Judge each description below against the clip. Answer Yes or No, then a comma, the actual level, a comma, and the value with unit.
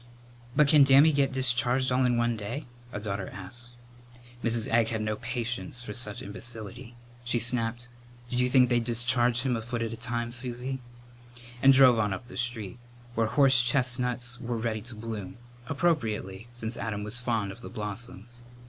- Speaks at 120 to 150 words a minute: No, average, 175 wpm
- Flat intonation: Yes, narrow, 2.0 semitones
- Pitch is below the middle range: Yes, low, 120 Hz